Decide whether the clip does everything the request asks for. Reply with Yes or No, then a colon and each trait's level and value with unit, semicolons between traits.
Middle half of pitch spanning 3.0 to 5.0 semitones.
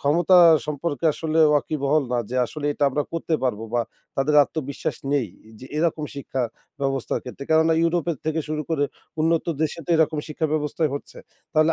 No: narrow, 2.4 semitones